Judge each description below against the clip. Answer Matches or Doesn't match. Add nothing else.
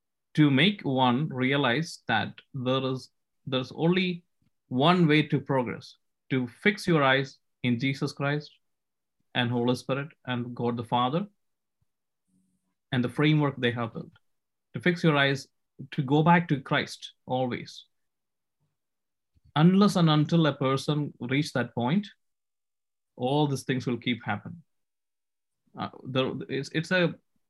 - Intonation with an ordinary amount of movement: Matches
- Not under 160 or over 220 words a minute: Doesn't match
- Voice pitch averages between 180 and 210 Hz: Doesn't match